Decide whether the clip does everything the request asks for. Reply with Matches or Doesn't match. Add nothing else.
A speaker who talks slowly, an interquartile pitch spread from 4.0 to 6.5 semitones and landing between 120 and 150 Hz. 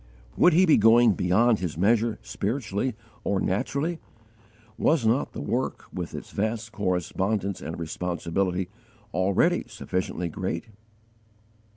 Doesn't match